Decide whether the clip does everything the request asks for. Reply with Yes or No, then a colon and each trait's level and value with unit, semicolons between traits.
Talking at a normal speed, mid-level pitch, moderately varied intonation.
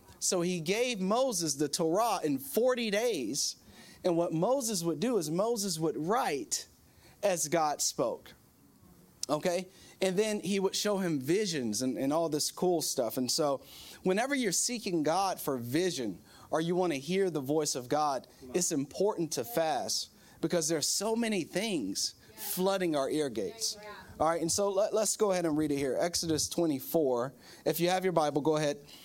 Yes: average, 180 wpm; medium, 175 Hz; average, 4.7 semitones